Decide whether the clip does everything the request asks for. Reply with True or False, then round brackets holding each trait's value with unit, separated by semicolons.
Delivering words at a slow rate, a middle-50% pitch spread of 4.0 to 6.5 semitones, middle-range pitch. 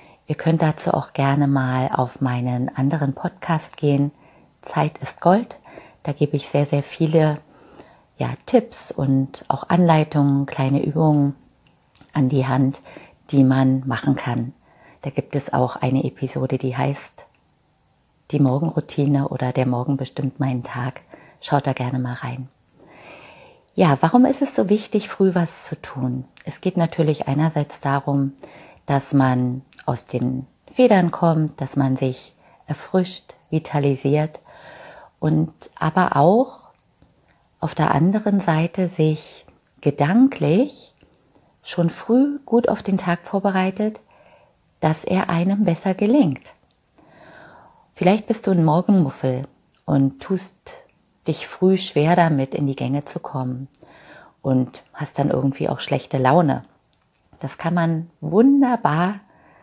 True (130 wpm; 4.8 semitones; 150 Hz)